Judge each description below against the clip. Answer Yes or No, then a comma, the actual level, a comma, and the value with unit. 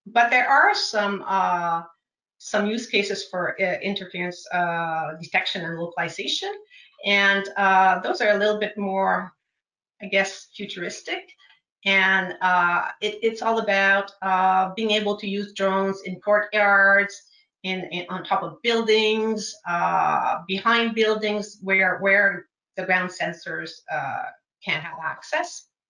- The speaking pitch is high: Yes, high, 200 Hz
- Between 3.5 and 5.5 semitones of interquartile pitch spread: No, narrow, 2.5 semitones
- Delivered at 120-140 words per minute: Yes, slow, 135 wpm